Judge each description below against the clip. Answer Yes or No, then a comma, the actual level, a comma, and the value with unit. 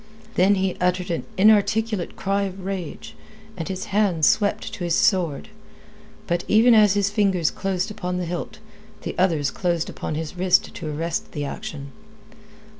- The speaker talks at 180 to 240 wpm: No, average, 160 wpm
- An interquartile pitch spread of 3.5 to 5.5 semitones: No, average, 2.9 semitones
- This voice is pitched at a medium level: Yes, medium, 180 Hz